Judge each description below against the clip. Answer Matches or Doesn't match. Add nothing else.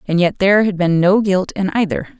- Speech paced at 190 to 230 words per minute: Doesn't match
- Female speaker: Matches